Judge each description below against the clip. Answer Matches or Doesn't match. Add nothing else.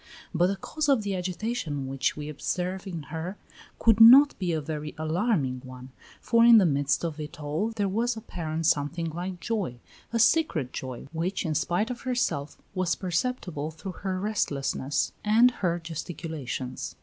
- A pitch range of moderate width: Doesn't match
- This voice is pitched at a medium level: Matches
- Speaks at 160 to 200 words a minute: Matches